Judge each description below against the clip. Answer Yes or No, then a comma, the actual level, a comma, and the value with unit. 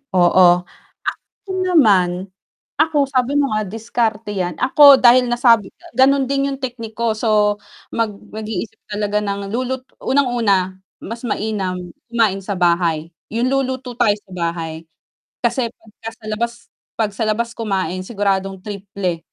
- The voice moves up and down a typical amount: Yes, average, 4.0 semitones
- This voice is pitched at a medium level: No, high, 215 Hz